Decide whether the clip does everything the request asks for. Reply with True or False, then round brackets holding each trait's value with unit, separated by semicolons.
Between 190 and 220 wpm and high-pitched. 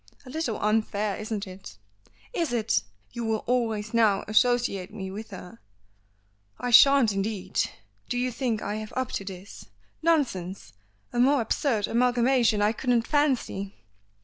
False (145 wpm; 225 Hz)